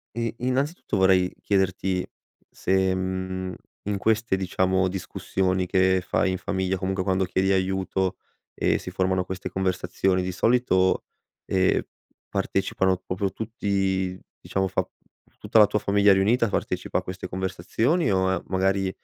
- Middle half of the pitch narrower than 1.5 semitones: Yes, narrow, 0.9 semitones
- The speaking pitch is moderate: No, very low, 95 Hz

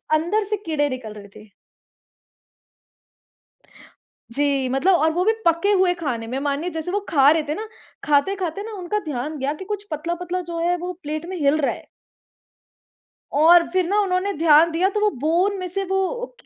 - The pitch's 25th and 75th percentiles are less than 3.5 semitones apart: No, average, 4.4 semitones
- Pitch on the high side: Yes, very high, 335 Hz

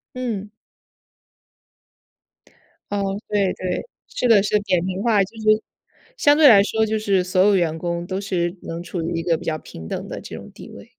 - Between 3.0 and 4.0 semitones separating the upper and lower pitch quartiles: Yes, average, 3.6 semitones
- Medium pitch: No, high, 195 Hz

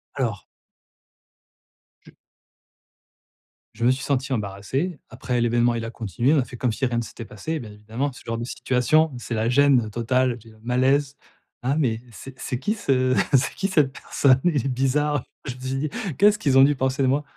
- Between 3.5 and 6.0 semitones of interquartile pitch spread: No, average, 2.9 semitones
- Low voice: Yes, low, 130 Hz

